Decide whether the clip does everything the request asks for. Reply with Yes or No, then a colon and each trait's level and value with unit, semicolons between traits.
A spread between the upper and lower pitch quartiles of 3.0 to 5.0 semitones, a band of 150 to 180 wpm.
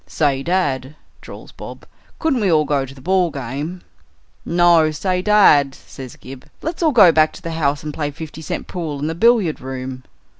No: average, 4.6 semitones; average, 190 wpm